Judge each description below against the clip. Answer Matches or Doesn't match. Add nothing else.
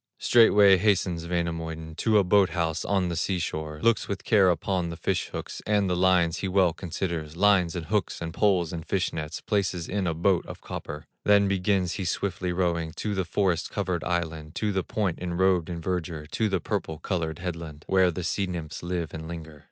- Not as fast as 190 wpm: Doesn't match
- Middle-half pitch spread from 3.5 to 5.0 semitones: Doesn't match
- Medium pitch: Doesn't match